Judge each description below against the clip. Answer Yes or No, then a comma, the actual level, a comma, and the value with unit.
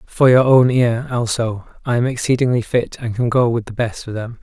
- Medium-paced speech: No, fast, 230 wpm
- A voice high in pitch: No, low, 120 Hz